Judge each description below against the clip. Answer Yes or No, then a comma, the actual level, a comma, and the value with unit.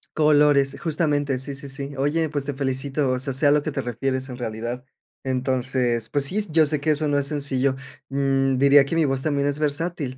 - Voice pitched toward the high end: No, medium, 140 Hz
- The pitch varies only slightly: Yes, narrow, 1.9 semitones